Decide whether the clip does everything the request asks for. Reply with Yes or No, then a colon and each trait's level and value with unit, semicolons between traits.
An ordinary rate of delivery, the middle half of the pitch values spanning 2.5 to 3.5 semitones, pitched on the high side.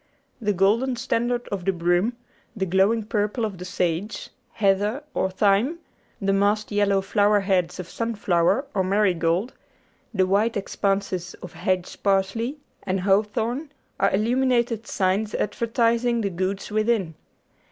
No: slow, 130 wpm; average, 3.2 semitones; high, 205 Hz